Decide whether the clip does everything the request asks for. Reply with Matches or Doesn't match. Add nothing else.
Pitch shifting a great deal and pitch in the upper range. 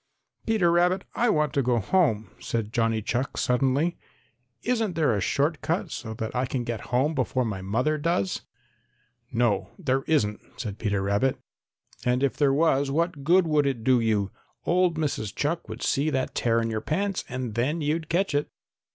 Doesn't match